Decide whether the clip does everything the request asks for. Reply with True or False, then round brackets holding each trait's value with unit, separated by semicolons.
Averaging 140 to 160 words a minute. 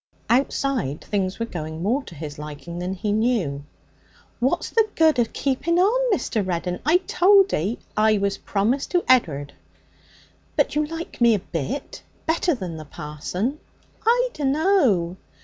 True (150 wpm)